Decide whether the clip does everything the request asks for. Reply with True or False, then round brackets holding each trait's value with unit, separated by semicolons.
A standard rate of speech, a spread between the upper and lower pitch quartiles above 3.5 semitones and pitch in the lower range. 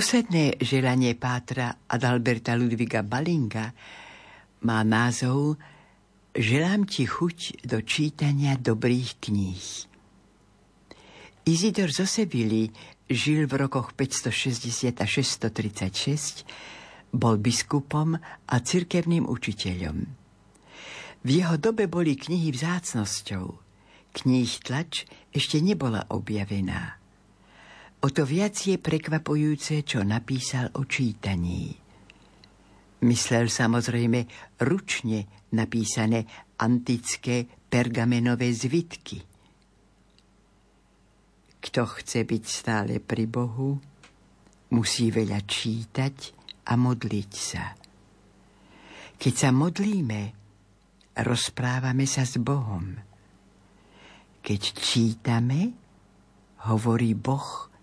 False (80 wpm; 4.2 semitones; 120 Hz)